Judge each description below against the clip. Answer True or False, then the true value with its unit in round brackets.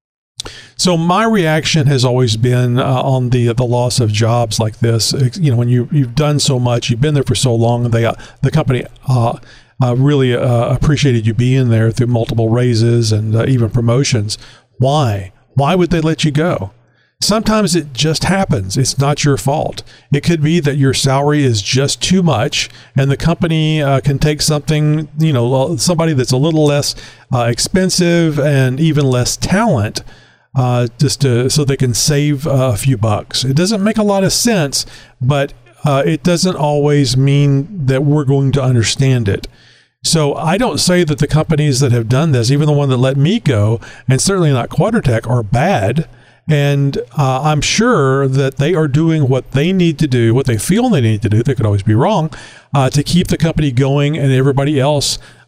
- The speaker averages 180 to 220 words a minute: True (195 wpm)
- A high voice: False (135 Hz)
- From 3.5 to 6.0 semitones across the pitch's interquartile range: True (3.9 semitones)